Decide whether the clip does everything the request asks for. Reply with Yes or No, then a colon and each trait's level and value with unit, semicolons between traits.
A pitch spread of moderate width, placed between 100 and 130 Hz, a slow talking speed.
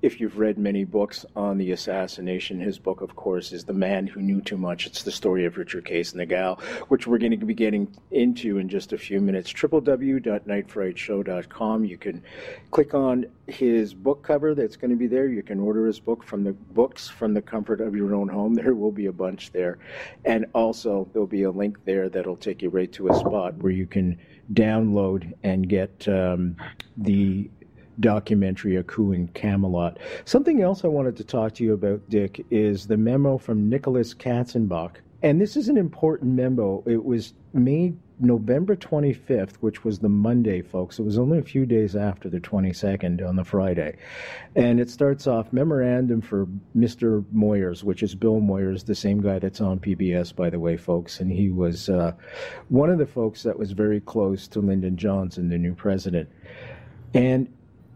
No: average, 3.9 semitones; low, 105 Hz; average, 195 wpm